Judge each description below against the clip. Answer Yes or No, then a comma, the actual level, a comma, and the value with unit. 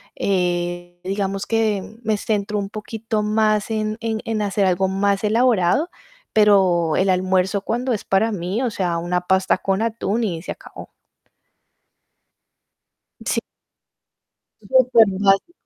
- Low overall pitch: No, high, 200 Hz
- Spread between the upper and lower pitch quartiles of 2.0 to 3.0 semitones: Yes, average, 2.7 semitones